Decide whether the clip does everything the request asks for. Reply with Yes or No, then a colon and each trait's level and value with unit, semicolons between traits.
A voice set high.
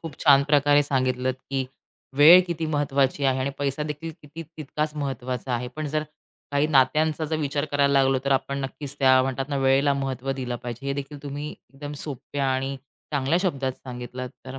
No: medium, 140 Hz